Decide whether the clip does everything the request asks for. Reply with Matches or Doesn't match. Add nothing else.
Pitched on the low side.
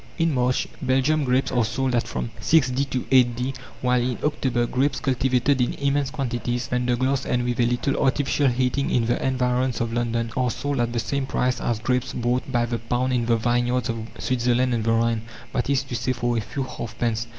Matches